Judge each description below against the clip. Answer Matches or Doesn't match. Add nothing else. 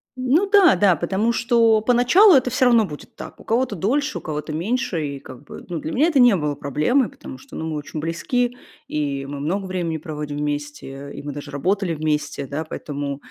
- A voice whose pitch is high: Doesn't match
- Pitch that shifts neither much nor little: Doesn't match